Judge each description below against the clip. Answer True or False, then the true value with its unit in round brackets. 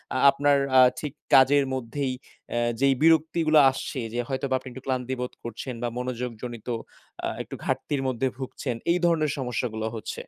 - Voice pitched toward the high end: False (130 Hz)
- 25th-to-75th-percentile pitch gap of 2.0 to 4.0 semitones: True (2.6 semitones)